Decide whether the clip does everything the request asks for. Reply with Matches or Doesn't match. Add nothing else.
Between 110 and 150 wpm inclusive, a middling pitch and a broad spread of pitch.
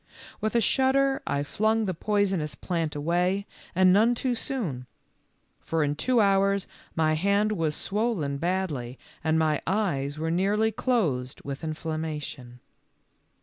Matches